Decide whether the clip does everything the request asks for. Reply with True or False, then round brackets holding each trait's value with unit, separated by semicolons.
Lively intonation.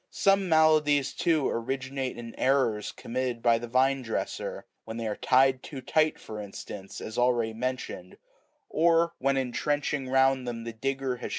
False (3.0 semitones)